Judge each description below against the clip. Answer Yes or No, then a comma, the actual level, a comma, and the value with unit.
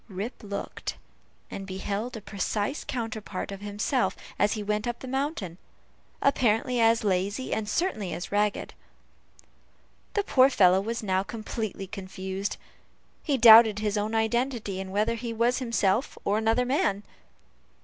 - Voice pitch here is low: No, high, 215 Hz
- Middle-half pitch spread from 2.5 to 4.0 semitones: Yes, average, 3.1 semitones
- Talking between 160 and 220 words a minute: No, average, 140 wpm